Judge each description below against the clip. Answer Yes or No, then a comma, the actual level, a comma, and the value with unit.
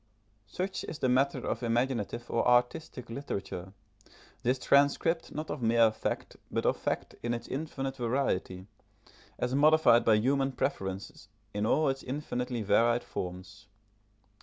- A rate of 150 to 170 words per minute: No, slow, 135 wpm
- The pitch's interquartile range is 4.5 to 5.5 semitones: No, average, 3.5 semitones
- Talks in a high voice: No, low, 125 Hz